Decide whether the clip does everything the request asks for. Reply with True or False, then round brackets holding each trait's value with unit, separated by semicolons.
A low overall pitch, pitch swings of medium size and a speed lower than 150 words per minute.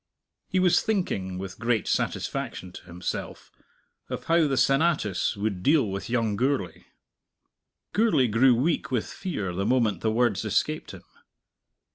False (115 Hz; 6.8 semitones; 140 wpm)